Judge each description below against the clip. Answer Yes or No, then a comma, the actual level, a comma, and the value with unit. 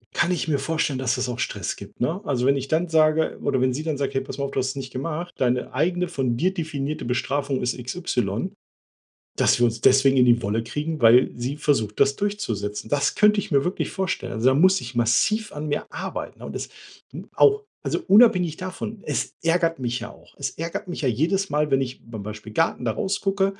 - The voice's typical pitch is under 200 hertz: Yes, medium, 140 Hz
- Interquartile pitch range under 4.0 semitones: No, average, 5.2 semitones